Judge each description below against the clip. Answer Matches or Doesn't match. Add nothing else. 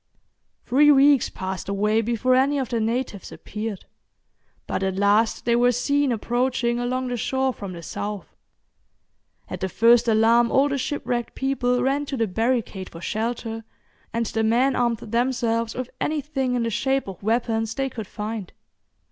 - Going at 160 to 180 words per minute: Matches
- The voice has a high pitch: Matches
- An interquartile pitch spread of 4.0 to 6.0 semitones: Doesn't match